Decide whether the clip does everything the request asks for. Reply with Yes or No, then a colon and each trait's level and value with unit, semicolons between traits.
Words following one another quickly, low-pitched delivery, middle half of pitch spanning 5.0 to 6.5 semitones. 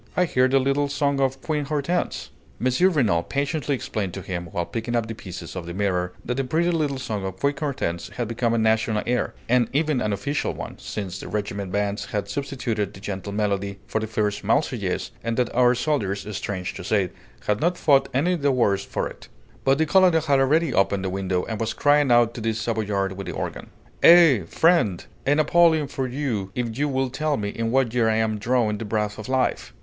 Yes: fast, 215 wpm; low, 115 Hz; wide, 5.6 semitones